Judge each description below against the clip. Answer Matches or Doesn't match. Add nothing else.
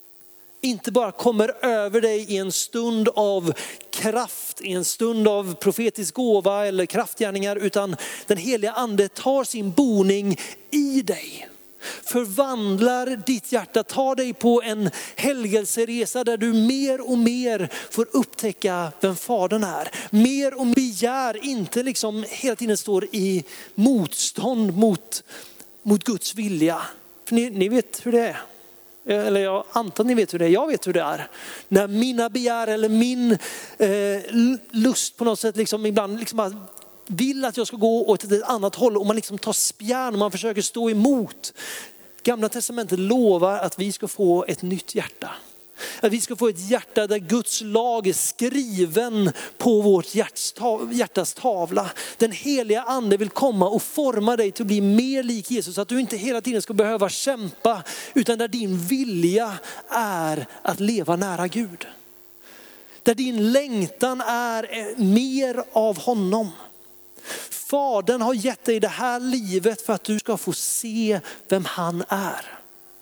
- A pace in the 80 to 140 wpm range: Doesn't match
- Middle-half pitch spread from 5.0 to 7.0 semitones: Doesn't match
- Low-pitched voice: Doesn't match